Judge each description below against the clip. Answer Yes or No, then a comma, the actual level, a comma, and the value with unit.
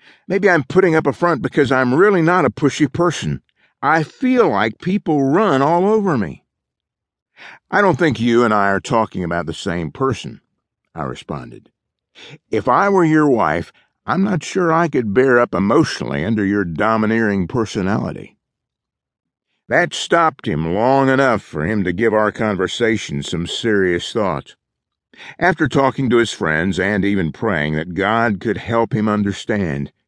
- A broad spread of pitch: Yes, wide, 8.2 semitones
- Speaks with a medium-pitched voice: No, low, 120 Hz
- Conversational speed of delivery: Yes, average, 160 wpm